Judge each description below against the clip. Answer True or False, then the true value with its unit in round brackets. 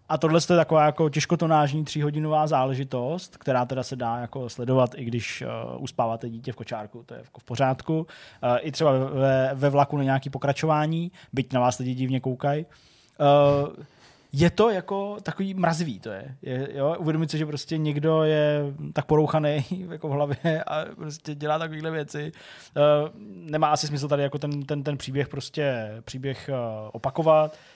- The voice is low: False (145 Hz)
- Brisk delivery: True (175 wpm)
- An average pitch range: True (3.0 semitones)